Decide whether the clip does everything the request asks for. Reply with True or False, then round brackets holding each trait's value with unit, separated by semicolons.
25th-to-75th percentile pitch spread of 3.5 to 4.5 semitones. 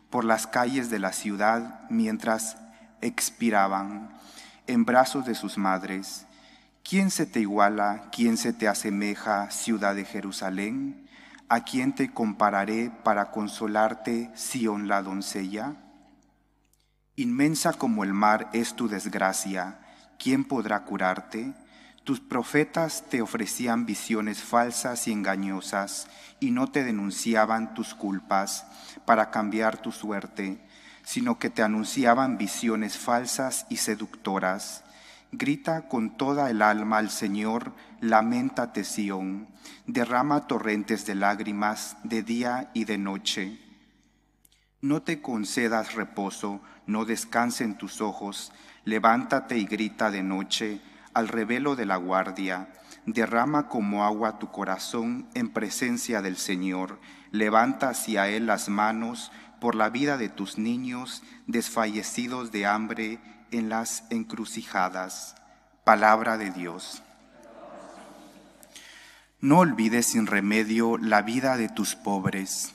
False (3.0 semitones)